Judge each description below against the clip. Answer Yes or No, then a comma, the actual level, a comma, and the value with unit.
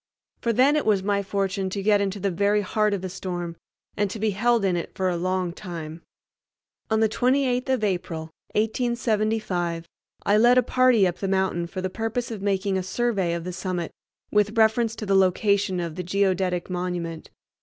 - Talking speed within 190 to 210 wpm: Yes, average, 195 wpm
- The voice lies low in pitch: No, high, 195 Hz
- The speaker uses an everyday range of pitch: Yes, average, 3.3 semitones